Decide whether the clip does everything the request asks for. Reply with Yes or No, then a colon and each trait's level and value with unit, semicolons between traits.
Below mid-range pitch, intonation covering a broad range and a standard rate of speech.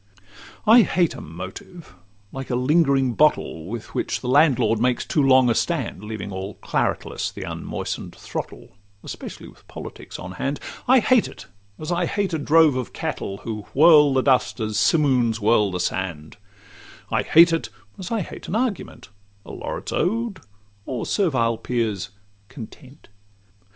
Yes: low, 130 Hz; wide, 7.0 semitones; average, 155 wpm